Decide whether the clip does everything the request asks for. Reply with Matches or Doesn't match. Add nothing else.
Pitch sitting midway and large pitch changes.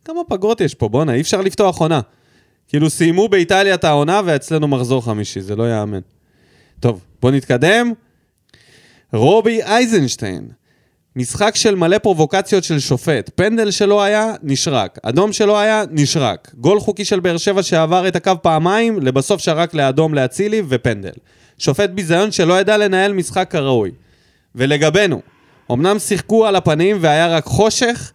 Matches